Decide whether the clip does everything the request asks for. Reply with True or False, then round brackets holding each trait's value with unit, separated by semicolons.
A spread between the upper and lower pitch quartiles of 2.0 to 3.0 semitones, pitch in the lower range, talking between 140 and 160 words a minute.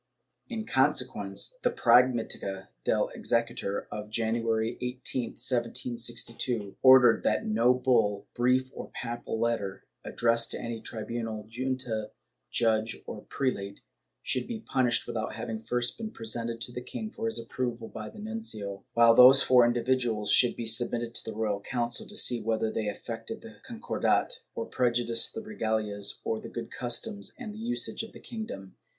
True (2.4 semitones; 115 Hz; 155 wpm)